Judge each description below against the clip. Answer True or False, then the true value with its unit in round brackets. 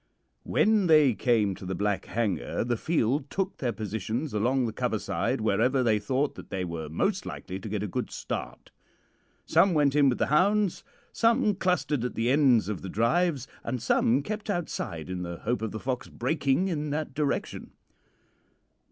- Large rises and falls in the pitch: True (6.4 semitones)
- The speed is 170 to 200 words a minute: True (180 wpm)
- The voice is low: True (130 Hz)